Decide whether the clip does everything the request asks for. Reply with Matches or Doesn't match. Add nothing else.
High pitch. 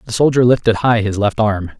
Doesn't match